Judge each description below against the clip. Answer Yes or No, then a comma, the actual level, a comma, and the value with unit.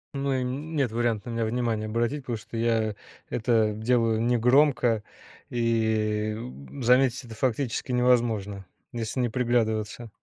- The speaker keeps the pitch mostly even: Yes, narrow, 2.2 semitones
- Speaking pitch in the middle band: No, low, 115 Hz